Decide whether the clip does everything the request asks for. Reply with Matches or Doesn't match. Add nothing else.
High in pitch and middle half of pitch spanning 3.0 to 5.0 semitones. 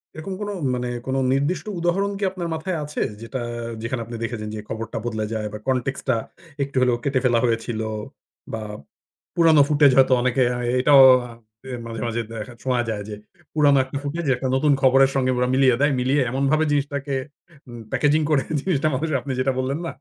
Doesn't match